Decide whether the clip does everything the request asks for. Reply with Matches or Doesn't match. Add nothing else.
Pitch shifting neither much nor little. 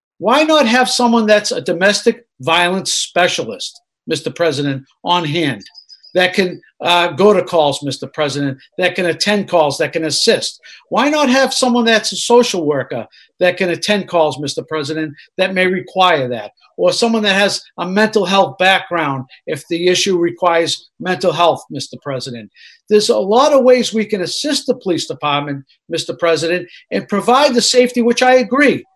Doesn't match